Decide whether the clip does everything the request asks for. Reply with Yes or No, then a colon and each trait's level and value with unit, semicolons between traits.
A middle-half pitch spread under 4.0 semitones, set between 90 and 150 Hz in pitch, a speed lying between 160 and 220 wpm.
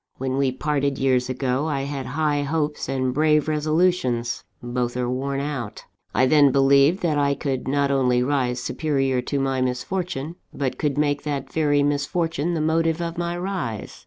Yes: average, 2.9 semitones; medium, 140 Hz; average, 170 wpm